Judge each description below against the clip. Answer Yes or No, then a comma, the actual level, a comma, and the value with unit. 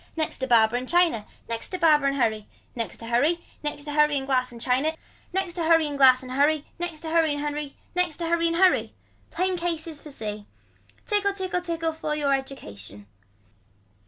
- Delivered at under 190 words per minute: No, average, 200 wpm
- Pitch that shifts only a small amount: No, average, 4.7 semitones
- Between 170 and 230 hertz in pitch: No, very high, 295 Hz